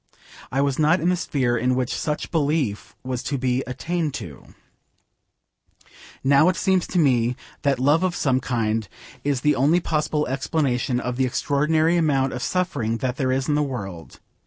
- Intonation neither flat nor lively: Yes, average, 3.6 semitones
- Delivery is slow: No, average, 175 wpm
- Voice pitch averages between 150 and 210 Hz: No, low, 135 Hz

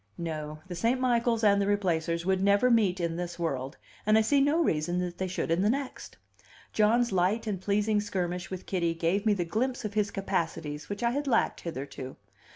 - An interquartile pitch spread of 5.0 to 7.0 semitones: No, average, 4.3 semitones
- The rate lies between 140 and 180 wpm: No, fast, 205 wpm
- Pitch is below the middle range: No, high, 195 Hz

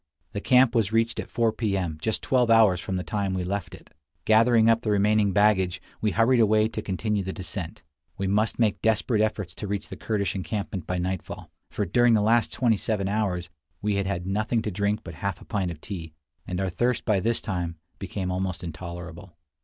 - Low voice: Yes, low, 100 Hz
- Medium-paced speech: No, fast, 210 wpm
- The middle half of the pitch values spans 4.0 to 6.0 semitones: No, average, 3.1 semitones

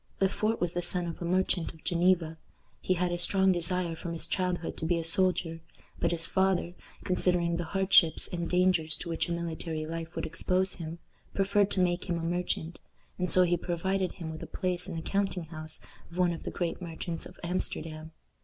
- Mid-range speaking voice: Yes, medium, 175 Hz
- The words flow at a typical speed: No, fast, 210 wpm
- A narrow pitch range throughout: Yes, narrow, 1.7 semitones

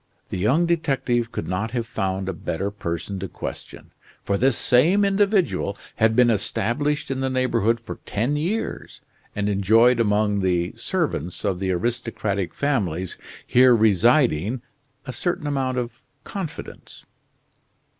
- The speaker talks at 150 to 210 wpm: No, slow, 135 wpm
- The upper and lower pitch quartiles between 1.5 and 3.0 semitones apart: No, average, 5.1 semitones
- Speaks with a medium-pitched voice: No, low, 115 Hz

